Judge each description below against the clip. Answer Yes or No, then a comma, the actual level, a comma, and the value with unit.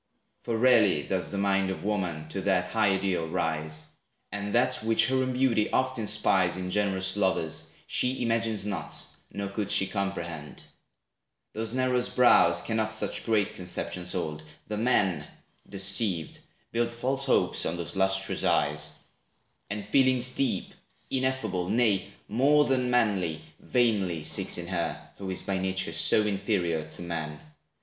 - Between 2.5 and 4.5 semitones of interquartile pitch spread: Yes, average, 4.2 semitones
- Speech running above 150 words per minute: No, average, 145 wpm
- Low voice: Yes, low, 100 Hz